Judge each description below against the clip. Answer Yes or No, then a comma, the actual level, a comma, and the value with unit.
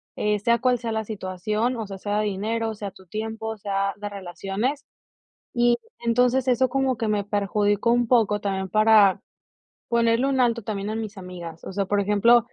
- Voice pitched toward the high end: Yes, high, 215 Hz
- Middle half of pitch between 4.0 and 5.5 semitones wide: No, average, 2.8 semitones